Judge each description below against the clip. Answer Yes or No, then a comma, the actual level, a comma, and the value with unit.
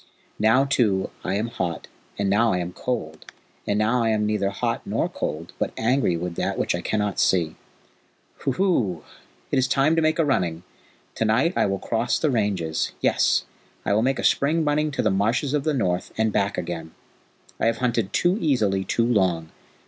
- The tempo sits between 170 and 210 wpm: Yes, average, 195 wpm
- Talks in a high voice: No, low, 110 Hz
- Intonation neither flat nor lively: No, wide, 5.8 semitones